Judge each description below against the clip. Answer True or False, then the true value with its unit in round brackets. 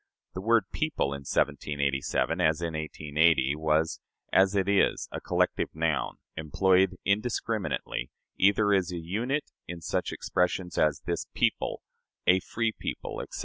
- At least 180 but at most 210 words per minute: False (140 wpm)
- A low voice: True (90 Hz)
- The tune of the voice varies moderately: True (4.3 semitones)